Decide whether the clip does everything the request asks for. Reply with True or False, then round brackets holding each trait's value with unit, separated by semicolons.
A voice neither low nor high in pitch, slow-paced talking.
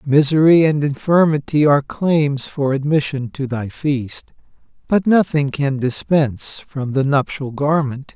True (145 Hz; 130 wpm)